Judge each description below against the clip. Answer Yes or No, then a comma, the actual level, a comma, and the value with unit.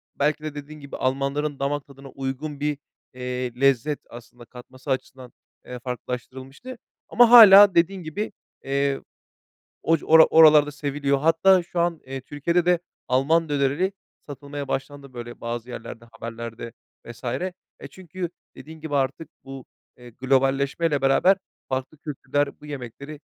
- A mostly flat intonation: No, average, 3.3 semitones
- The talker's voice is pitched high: No, medium, 140 Hz